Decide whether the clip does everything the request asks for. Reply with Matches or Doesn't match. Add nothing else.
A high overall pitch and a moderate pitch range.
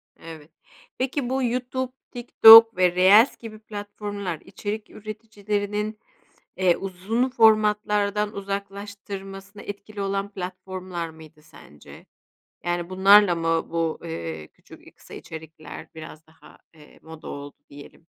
Matches